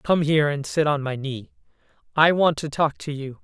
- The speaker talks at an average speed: No, fast, 225 wpm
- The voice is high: No, medium, 150 Hz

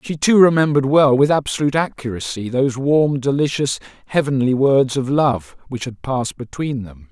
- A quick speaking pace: No, average, 160 wpm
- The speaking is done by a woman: No, male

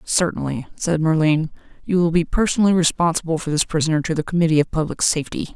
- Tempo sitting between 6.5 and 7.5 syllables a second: Yes, 6.6 syllables/s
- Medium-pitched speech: Yes, medium, 160 Hz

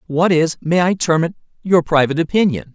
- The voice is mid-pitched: Yes, medium, 165 Hz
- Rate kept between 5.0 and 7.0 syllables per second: Yes, 5.7 syllables/s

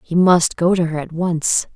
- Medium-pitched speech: Yes, medium, 170 Hz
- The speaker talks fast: Yes, fast, 240 wpm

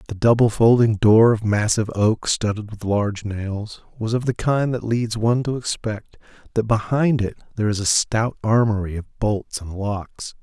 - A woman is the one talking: No, male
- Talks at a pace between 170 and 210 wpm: Yes, average, 185 wpm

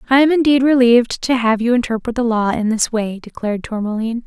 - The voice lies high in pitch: Yes, high, 235 Hz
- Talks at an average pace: No, fast, 210 wpm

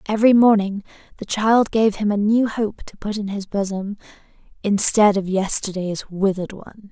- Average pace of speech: Yes, average, 165 wpm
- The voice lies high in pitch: Yes, high, 205 Hz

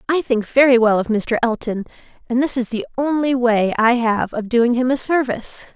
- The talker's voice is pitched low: No, high, 245 Hz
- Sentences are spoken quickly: Yes, fast, 210 wpm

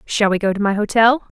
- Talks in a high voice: Yes, high, 215 Hz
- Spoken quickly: Yes, fast, 255 wpm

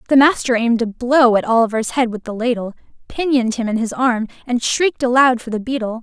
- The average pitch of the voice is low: No, high, 240 Hz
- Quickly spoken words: Yes, fast, 220 wpm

